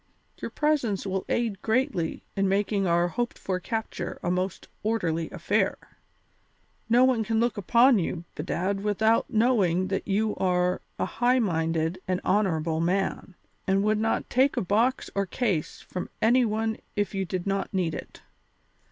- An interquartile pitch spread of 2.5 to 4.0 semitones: Yes, average, 3.7 semitones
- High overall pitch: Yes, high, 195 Hz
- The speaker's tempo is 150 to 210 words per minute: Yes, average, 160 wpm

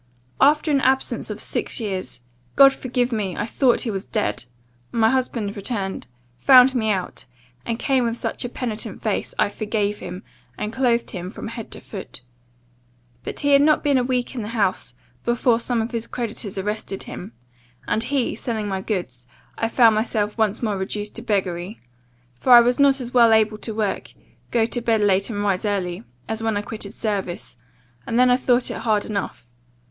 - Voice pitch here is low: No, high, 225 Hz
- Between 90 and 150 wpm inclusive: No, average, 190 wpm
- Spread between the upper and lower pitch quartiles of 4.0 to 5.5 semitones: No, average, 3.1 semitones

